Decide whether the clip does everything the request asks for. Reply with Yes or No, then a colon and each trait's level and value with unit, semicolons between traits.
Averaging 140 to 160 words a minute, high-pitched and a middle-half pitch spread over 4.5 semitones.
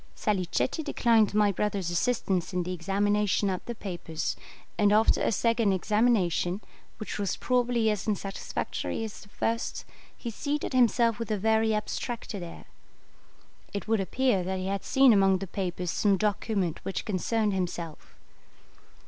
No: average, 150 wpm; high, 205 Hz; average, 3.2 semitones